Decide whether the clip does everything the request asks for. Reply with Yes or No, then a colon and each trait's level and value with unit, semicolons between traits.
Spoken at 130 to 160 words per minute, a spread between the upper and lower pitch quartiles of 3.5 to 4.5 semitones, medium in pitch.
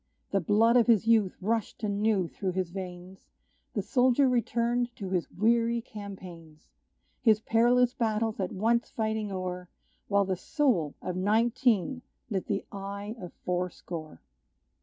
No: average, 140 wpm; average, 3.9 semitones; high, 210 Hz